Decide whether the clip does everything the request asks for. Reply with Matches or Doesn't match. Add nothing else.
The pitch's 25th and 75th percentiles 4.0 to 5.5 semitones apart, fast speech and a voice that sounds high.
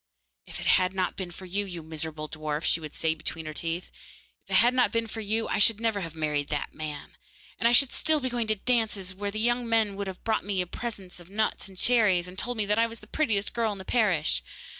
Matches